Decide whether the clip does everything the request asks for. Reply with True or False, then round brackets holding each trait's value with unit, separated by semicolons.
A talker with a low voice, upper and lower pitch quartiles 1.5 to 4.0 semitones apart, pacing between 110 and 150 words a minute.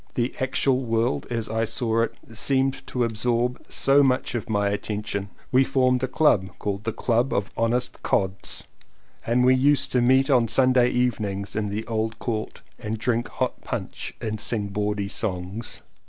False (115 Hz; 3.1 semitones; 175 wpm)